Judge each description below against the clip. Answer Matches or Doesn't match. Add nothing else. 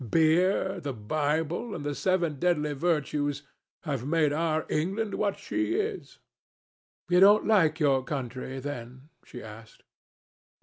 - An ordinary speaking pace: Doesn't match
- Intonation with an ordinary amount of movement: Matches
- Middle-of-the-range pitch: Matches